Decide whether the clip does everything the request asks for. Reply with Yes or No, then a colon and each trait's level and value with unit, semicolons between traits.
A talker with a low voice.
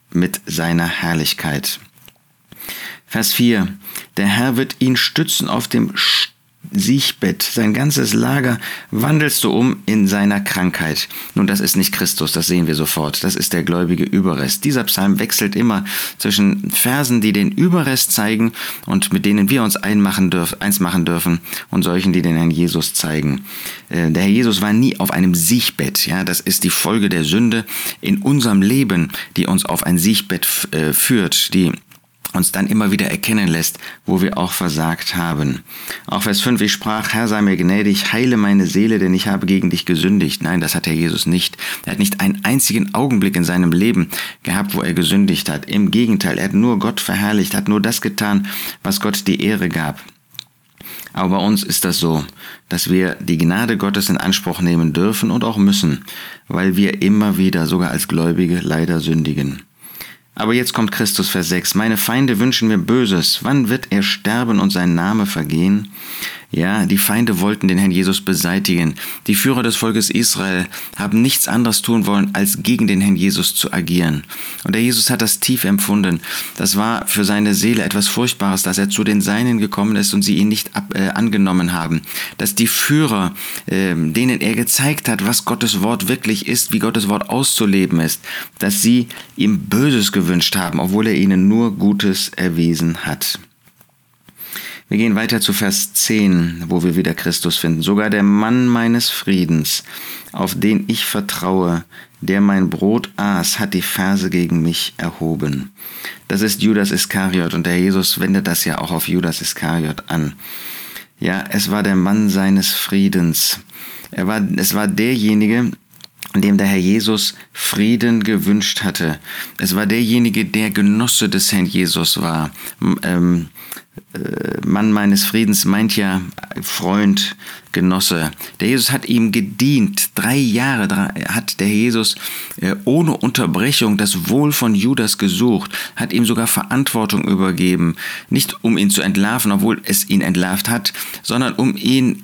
Yes: low, 100 Hz